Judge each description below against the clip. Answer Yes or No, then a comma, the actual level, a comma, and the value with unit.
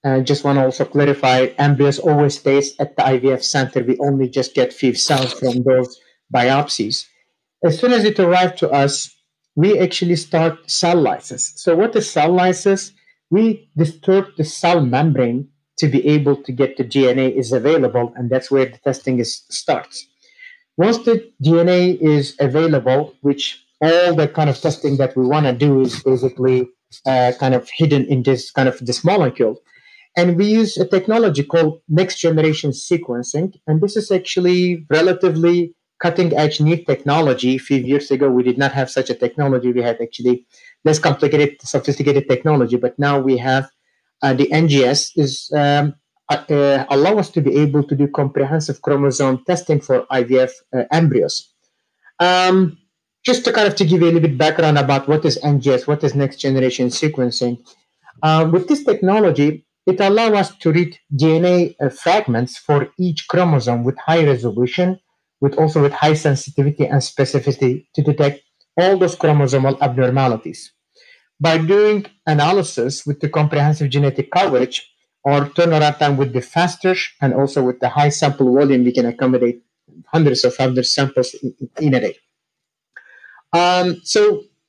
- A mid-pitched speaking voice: Yes, medium, 145 Hz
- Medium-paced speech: Yes, average, 165 wpm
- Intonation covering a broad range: No, average, 4.5 semitones